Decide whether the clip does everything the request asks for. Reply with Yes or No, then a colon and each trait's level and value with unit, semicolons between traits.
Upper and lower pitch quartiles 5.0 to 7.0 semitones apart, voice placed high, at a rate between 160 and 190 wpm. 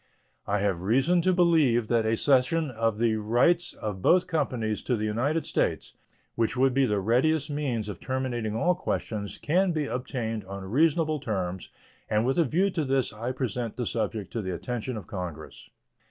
No: wide, 5.4 semitones; low, 120 Hz; average, 185 wpm